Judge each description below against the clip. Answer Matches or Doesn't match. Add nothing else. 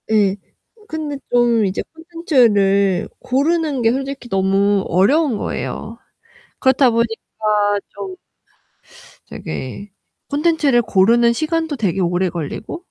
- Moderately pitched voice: Doesn't match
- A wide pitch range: Matches